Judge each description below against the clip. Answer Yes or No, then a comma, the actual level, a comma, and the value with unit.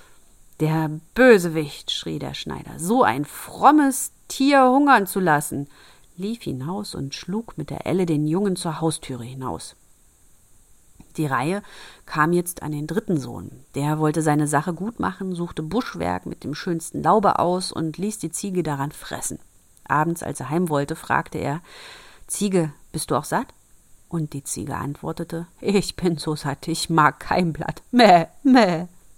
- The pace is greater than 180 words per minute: No, average, 160 wpm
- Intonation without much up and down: No, average, 4.7 semitones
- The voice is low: No, medium, 165 Hz